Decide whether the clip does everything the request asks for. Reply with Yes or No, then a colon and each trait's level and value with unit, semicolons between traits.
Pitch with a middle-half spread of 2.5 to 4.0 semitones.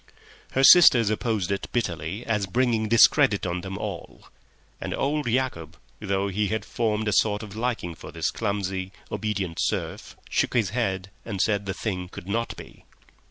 Yes: average, 3.2 semitones